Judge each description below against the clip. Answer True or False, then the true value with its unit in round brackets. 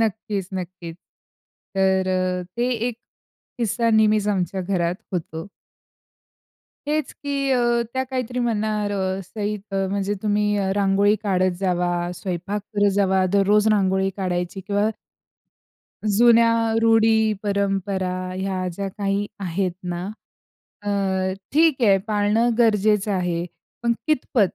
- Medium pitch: False (200 Hz)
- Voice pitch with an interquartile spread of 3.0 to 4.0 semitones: False (2.5 semitones)